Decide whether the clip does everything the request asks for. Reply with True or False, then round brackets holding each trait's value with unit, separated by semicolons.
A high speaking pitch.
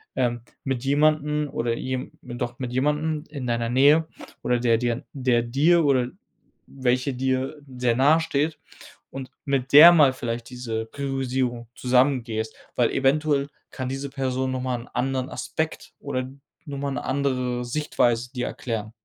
False (130 Hz)